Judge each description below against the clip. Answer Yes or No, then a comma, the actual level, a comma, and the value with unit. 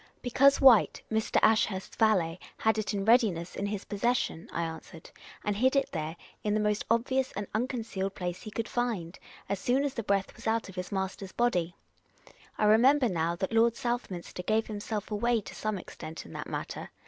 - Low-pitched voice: No, high, 210 Hz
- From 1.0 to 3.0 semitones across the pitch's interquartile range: No, average, 3.8 semitones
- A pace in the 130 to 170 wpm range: No, average, 200 wpm